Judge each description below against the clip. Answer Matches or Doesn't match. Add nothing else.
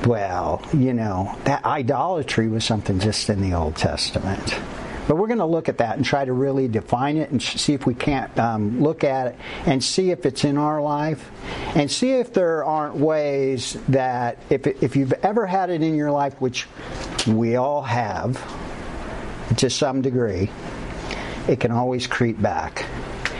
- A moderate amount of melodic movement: Matches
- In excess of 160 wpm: Matches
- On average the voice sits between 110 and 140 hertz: Matches